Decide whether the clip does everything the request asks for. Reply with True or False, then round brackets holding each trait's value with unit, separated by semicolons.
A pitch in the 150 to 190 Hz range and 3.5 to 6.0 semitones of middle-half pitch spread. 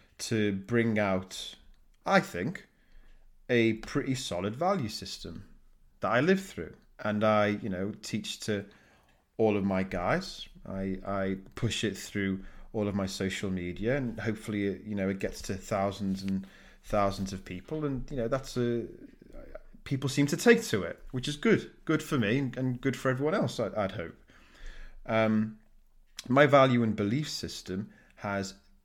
False (105 Hz; 4.3 semitones)